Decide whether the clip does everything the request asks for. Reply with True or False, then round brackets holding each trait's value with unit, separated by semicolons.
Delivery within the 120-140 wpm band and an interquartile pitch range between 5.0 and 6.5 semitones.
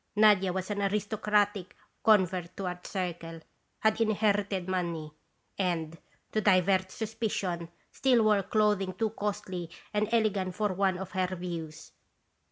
False (135 wpm; 2.7 semitones)